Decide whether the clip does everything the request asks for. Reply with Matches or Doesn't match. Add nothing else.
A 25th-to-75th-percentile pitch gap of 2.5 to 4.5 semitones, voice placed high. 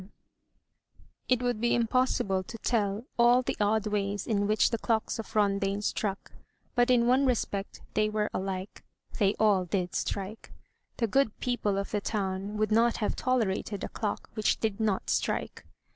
Matches